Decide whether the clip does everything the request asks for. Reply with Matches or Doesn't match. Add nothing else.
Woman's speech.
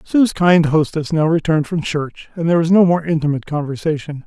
Doesn't match